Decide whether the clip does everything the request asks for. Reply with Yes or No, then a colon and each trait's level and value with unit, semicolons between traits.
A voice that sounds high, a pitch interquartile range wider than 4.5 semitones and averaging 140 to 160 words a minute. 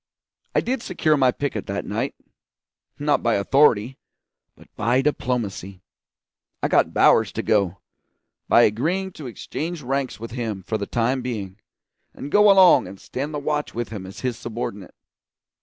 No: low, 125 Hz; wide, 5.6 semitones; average, 155 wpm